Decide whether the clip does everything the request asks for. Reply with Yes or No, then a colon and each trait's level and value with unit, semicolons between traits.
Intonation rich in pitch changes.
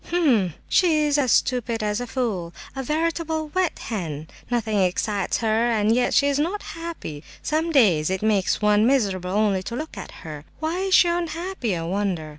Yes: wide, 8.1 semitones